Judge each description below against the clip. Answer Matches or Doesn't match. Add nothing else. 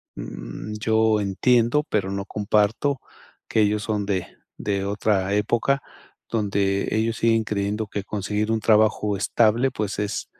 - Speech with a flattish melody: Matches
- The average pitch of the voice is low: Matches